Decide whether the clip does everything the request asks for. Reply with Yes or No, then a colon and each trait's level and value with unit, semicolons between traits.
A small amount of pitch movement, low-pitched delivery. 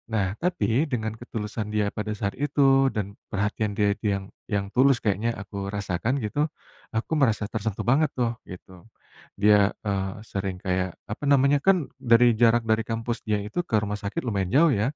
No: average, 3.0 semitones; low, 110 Hz